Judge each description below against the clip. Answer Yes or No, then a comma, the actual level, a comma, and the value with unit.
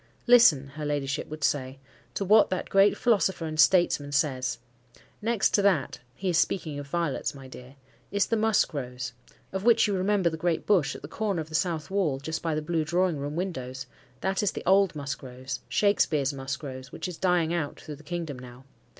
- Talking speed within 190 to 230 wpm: Yes, average, 195 wpm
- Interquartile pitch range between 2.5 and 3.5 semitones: No, wide, 5.4 semitones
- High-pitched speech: No, medium, 155 Hz